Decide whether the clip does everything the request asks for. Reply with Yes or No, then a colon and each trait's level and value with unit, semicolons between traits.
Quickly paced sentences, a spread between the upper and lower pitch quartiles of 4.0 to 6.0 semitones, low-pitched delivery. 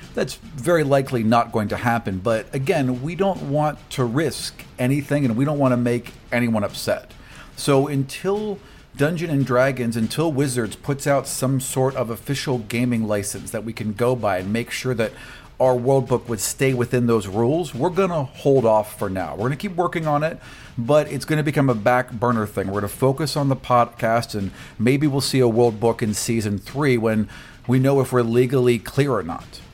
No: fast, 210 wpm; average, 3.3 semitones; low, 125 Hz